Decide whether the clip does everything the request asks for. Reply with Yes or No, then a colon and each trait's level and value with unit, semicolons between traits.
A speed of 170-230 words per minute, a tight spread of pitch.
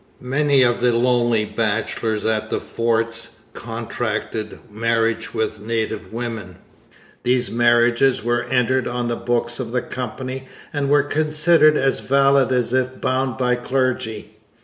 No: slow, 135 wpm; narrow, 2.3 semitones